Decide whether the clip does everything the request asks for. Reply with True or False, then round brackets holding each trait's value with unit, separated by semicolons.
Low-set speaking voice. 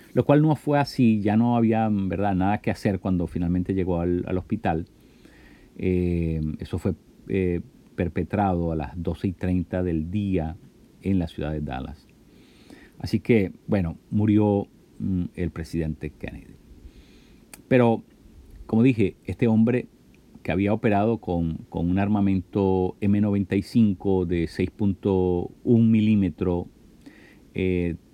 True (95 Hz)